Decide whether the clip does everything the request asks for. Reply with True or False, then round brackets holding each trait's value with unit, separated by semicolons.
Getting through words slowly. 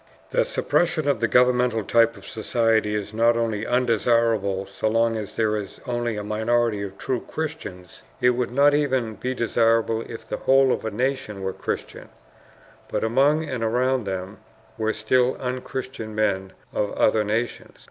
False (165 wpm)